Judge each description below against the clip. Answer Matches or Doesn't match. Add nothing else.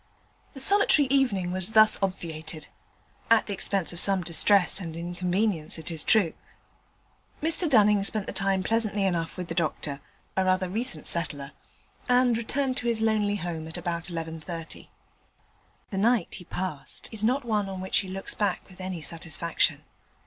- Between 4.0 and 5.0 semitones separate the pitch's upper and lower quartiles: Matches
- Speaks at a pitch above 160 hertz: Matches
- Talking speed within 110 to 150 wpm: Doesn't match